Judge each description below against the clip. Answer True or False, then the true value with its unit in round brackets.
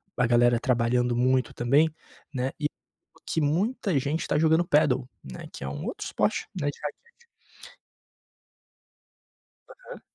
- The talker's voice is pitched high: False (140 Hz)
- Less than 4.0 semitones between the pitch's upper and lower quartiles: False (4.6 semitones)